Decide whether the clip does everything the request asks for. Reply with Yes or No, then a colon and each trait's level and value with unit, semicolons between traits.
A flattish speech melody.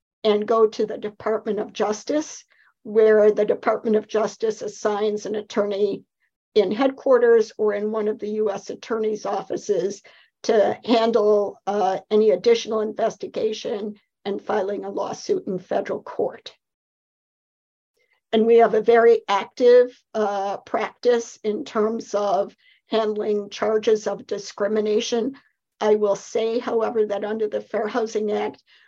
Yes: narrow, 1.9 semitones